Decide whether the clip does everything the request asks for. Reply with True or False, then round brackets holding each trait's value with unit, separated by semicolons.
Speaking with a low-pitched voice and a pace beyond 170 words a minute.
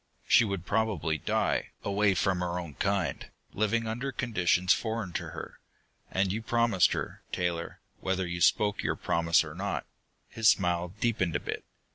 False (95 Hz; 160 wpm)